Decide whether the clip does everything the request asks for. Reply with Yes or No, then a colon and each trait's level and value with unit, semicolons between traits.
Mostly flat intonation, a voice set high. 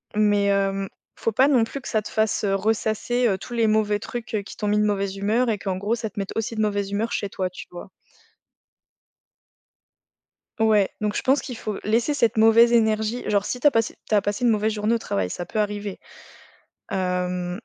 Yes: narrow, 2.3 semitones; high, 210 Hz